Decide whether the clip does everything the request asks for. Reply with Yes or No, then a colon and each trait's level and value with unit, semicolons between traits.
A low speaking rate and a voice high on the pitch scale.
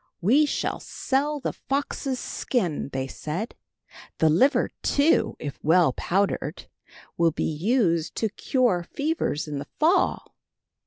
Yes: slow, 125 wpm; high, 200 Hz